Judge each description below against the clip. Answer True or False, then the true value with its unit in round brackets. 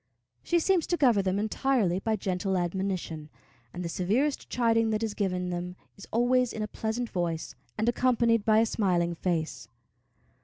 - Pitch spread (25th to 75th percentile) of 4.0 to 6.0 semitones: True (4.6 semitones)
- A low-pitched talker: False (210 Hz)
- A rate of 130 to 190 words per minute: True (165 wpm)